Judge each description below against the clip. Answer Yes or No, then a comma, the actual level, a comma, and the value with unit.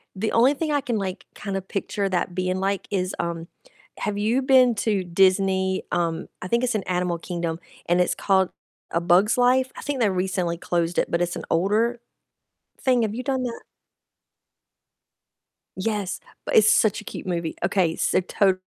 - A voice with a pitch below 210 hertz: Yes, high, 190 Hz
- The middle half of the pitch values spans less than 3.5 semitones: No, average, 4.1 semitones